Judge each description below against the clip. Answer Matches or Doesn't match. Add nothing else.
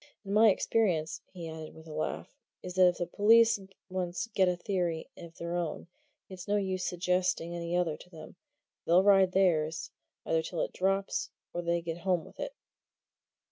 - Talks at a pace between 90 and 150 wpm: Doesn't match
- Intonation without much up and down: Matches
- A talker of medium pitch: Matches